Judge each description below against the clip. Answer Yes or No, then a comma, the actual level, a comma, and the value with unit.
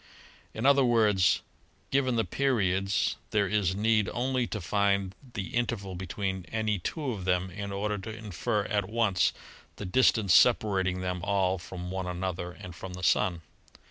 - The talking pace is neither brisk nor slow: Yes, average, 160 wpm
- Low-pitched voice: Yes, low, 100 Hz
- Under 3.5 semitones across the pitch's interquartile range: Yes, average, 3.1 semitones